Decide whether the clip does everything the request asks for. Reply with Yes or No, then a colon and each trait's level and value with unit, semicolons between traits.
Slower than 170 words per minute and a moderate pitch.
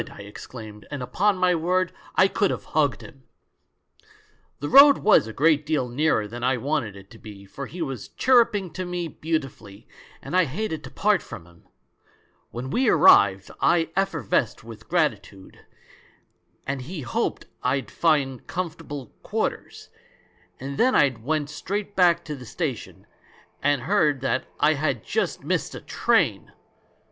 Yes: average, 155 wpm; medium, 145 Hz